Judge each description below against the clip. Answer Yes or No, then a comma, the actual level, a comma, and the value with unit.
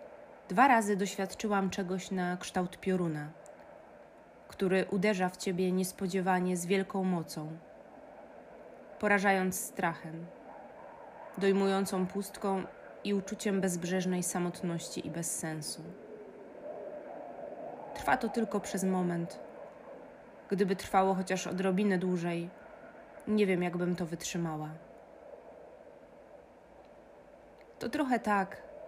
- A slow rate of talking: Yes, slow, 90 wpm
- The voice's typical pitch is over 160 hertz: Yes, high, 190 Hz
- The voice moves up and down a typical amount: No, narrow, 2.2 semitones